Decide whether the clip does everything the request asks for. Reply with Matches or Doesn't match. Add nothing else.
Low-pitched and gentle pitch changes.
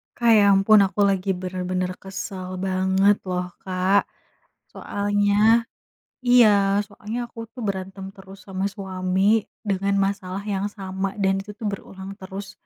Doesn't match